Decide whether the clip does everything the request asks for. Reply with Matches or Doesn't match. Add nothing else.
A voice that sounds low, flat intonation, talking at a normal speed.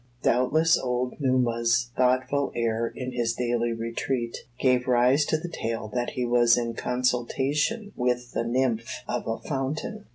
Matches